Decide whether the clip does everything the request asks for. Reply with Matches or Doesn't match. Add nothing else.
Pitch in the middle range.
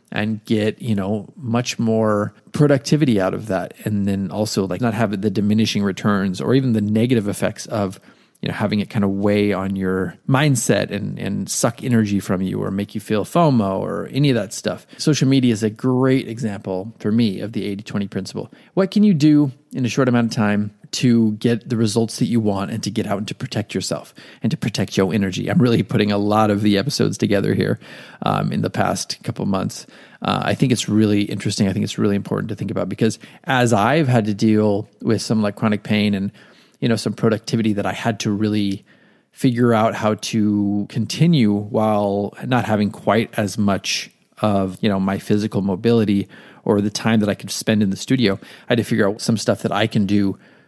Doesn't match